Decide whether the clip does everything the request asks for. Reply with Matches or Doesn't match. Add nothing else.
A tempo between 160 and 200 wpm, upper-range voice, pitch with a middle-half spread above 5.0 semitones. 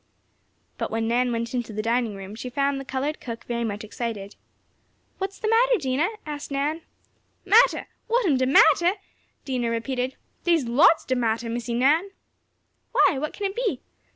Matches